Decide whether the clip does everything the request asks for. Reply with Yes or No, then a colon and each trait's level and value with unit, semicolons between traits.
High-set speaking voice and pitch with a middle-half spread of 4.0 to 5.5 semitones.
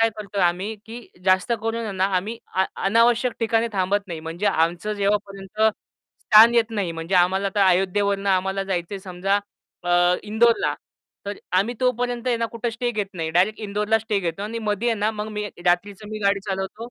No: high, 205 Hz; average, 3.0 semitones